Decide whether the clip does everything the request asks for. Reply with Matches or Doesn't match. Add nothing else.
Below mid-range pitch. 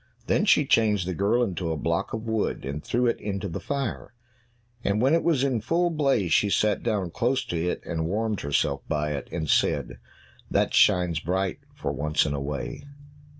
Matches